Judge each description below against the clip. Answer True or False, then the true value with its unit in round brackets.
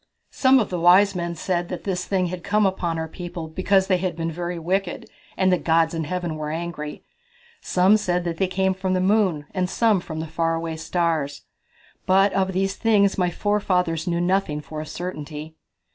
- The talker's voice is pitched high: False (180 Hz)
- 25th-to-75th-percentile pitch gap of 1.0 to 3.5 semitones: True (2.6 semitones)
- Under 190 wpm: False (195 wpm)